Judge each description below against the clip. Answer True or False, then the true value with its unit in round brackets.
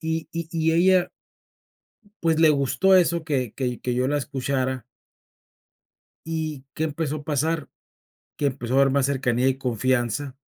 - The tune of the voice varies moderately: True (3.7 semitones)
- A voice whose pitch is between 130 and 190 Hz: True (140 Hz)